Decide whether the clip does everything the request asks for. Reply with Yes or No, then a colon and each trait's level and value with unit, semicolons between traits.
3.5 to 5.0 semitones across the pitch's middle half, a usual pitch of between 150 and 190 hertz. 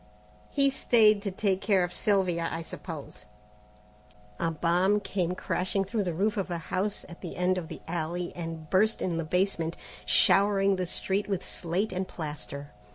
No: average, 2.9 semitones; medium, 185 Hz